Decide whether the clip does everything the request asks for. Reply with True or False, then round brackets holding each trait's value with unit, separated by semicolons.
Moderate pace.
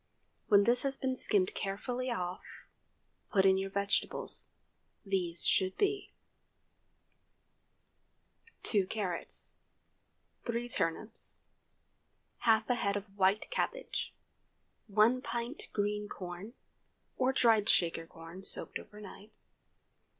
False (100 wpm)